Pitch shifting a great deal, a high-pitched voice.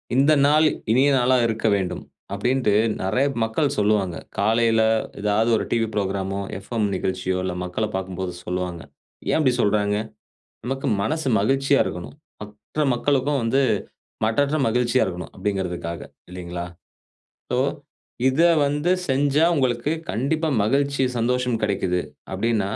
No: wide, 5.7 semitones; low, 110 Hz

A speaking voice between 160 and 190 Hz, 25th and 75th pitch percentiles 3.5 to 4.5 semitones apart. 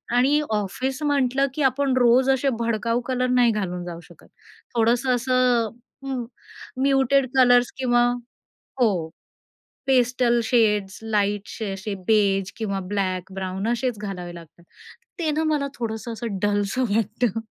No: high, 235 Hz; average, 3.9 semitones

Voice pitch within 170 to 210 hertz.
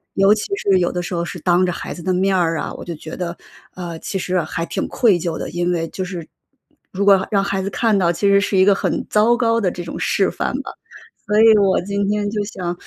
Yes: high, 190 Hz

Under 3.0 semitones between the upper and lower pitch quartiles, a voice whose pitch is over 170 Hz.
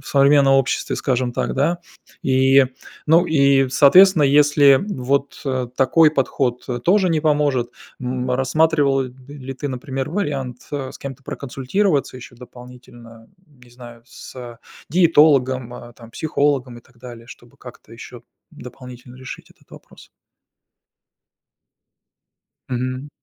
No: narrow, 2.5 semitones; low, 135 Hz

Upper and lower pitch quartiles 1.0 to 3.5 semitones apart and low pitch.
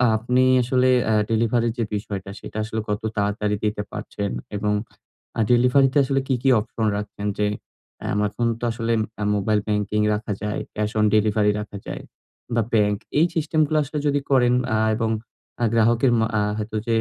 Yes: average, 2.9 semitones; low, 110 Hz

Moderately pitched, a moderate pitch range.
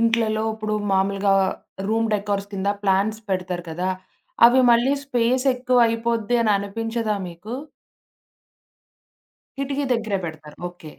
No: high, 215 Hz; average, 3.1 semitones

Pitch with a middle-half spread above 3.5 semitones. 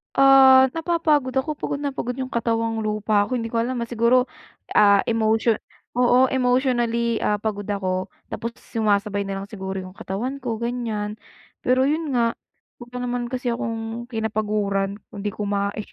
No: average, 3.2 semitones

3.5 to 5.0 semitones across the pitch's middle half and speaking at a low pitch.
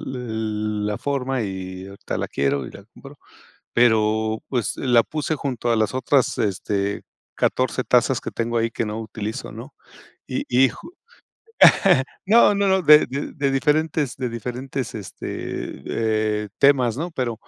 Yes: average, 4.2 semitones; low, 120 Hz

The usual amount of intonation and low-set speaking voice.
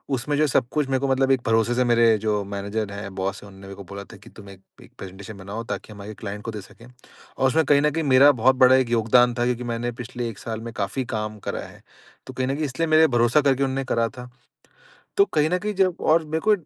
Yes: average, 4.1 semitones; low, 120 Hz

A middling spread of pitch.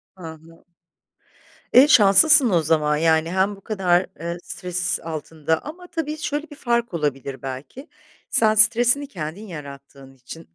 No: wide, 7.6 semitones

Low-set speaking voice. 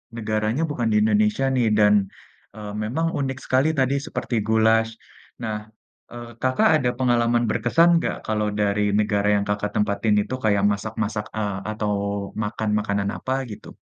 Yes: low, 110 Hz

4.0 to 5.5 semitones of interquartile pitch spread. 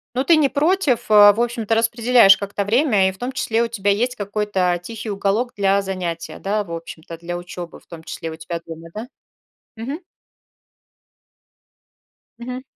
Yes: average, 4.5 semitones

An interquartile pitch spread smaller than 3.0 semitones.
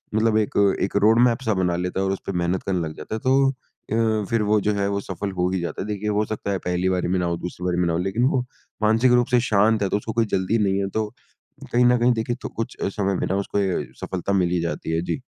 No: average, 3.3 semitones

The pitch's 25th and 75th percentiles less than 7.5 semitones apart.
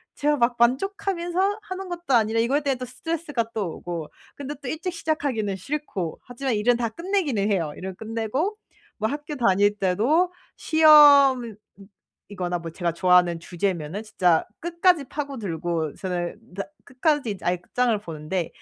No: wide, 7.9 semitones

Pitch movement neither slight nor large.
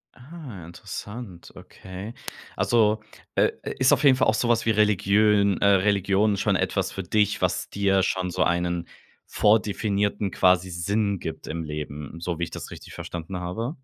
Yes: average, 3.3 semitones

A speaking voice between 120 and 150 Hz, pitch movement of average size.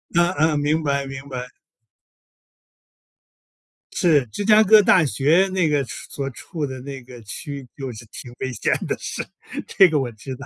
Yes: medium, 140 Hz; average, 3.7 semitones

